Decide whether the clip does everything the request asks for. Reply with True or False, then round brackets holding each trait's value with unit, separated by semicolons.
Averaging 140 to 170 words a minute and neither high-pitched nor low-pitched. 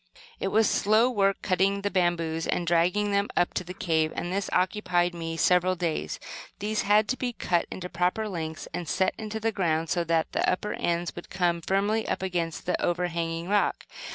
False (200 wpm; 180 Hz)